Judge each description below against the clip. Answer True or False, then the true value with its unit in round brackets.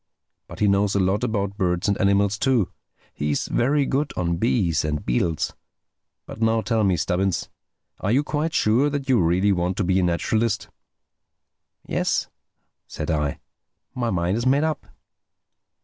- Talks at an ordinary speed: True (155 wpm)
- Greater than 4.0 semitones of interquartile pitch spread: True (5.0 semitones)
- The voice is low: True (100 Hz)